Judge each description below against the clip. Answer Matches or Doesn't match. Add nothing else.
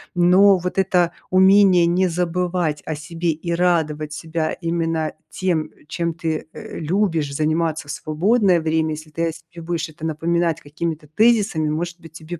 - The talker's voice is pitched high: Doesn't match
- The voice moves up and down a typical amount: Doesn't match